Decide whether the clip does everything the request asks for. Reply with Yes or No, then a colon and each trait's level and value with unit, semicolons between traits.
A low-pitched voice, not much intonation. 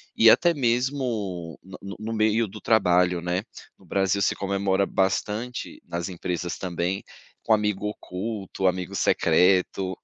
No: very low, 95 Hz; average, 3.1 semitones